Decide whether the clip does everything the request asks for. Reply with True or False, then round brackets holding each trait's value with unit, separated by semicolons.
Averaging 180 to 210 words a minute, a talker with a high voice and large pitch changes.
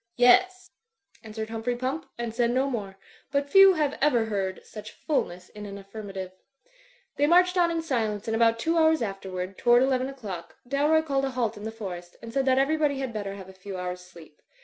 True (200 wpm; 235 Hz; 5.9 semitones)